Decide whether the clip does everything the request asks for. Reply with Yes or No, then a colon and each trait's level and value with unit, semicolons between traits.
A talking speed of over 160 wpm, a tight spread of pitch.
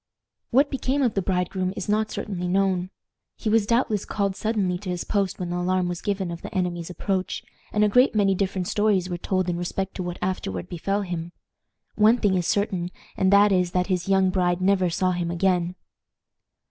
Yes: average, 200 wpm; narrow, 2.3 semitones